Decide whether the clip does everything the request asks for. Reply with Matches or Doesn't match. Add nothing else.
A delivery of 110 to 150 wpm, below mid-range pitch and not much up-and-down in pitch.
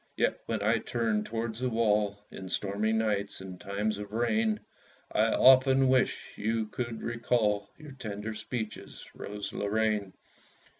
Matches